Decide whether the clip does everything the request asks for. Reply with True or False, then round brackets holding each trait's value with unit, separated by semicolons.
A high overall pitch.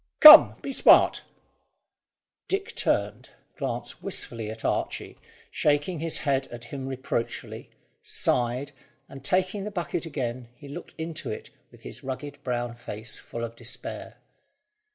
False (135 Hz)